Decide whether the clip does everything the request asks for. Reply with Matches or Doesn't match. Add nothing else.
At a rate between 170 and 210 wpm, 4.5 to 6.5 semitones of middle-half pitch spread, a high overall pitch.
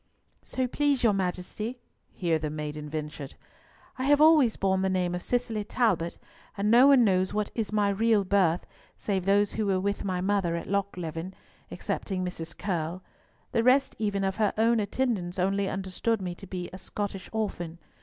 Doesn't match